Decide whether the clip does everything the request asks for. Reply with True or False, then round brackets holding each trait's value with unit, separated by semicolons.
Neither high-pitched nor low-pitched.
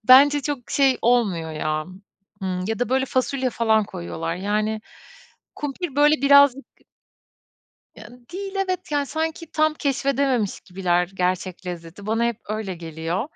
False (235 Hz)